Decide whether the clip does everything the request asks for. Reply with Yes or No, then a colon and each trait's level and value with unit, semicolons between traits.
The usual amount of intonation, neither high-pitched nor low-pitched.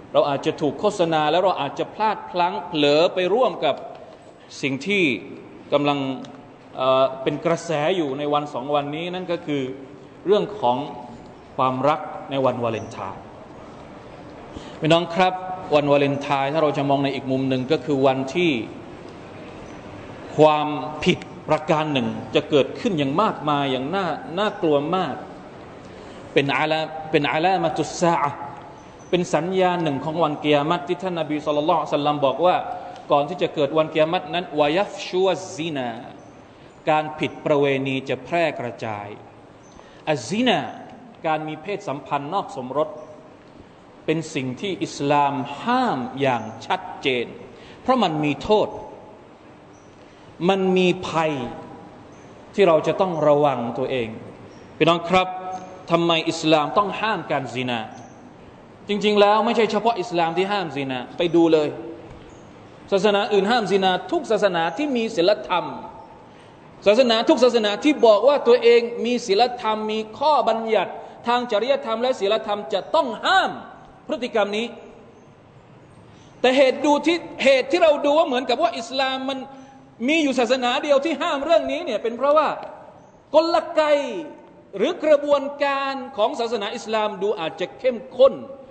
No: wide, 7.6 semitones; medium, 175 Hz